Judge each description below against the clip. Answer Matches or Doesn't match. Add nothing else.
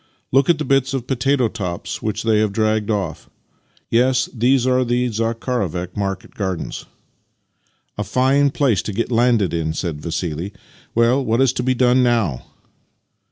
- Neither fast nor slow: Matches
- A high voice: Doesn't match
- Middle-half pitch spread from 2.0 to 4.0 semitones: Doesn't match